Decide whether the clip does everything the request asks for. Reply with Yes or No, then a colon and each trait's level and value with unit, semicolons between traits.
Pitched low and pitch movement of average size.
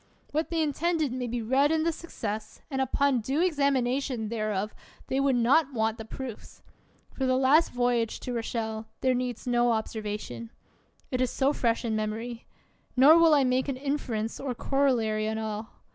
No: very high, 250 Hz; average, 3.8 semitones